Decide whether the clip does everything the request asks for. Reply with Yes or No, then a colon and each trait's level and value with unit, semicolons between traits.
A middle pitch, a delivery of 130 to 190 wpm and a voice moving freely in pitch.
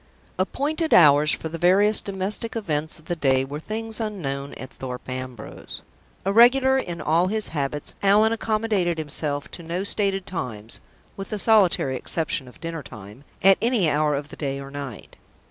Yes: medium, 170 Hz; average, 165 wpm; wide, 6.7 semitones